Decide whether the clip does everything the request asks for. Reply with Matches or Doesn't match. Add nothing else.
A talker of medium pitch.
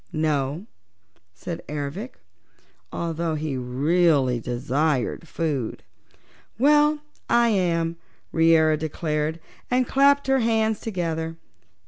Matches